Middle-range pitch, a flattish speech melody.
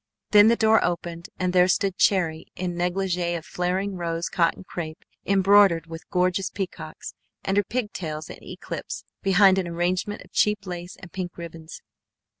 Yes: medium, 180 Hz; narrow, 2.3 semitones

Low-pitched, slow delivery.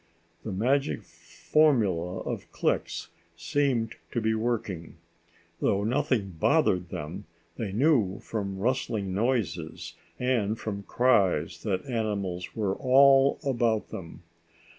Yes: low, 110 Hz; slow, 110 wpm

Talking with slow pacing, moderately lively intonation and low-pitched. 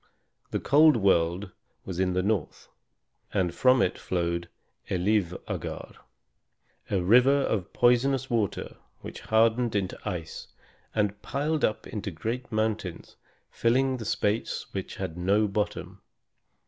Yes: slow, 120 wpm; average, 4.6 semitones; low, 105 Hz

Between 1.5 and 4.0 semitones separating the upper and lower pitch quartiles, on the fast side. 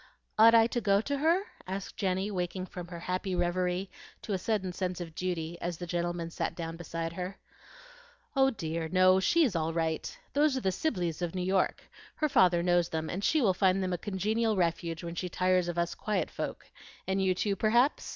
Yes: average, 2.8 semitones; fast, 210 wpm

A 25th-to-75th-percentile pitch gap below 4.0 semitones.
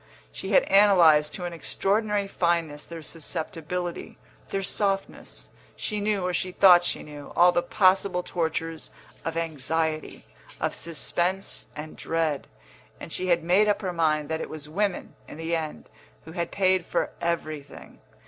Yes: average, 2.8 semitones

